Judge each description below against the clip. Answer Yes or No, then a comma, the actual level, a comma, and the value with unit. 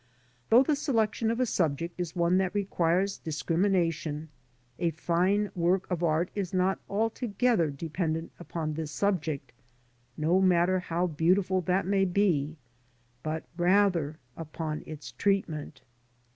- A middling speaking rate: No, slow, 130 wpm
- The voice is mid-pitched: Yes, medium, 175 Hz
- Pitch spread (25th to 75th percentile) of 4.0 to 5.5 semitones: No, average, 3.4 semitones